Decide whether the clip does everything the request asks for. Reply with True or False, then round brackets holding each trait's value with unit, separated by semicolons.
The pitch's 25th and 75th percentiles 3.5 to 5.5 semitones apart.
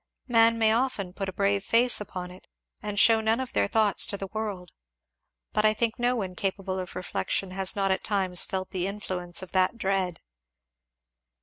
False (2.8 semitones)